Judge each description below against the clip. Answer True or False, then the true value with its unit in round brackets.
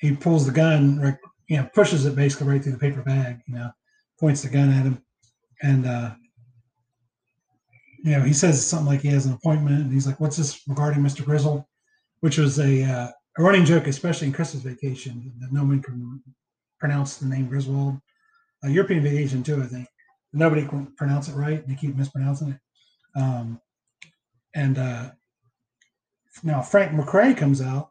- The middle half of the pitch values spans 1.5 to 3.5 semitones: True (2.7 semitones)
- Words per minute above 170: True (180 wpm)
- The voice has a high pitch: False (140 Hz)